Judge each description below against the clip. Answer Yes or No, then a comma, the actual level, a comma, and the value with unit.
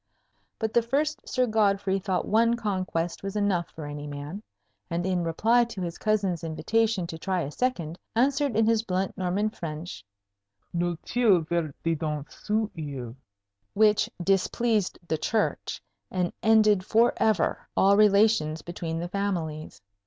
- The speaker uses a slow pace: No, average, 145 wpm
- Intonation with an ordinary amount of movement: Yes, average, 4.6 semitones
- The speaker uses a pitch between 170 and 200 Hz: Yes, high, 190 Hz